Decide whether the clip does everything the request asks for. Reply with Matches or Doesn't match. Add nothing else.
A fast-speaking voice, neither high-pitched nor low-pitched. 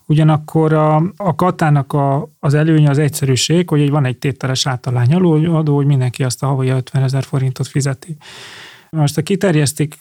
Matches